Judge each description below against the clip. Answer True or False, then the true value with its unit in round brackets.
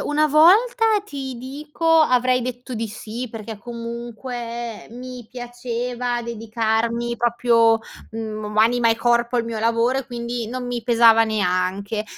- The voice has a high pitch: True (235 Hz)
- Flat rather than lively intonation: True (1.7 semitones)